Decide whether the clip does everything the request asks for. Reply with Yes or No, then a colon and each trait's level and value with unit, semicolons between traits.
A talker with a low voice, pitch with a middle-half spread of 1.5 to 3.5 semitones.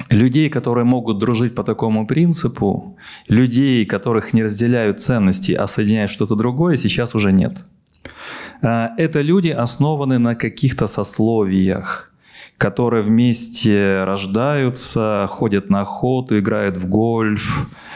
Yes: low, 115 Hz; average, 3.1 semitones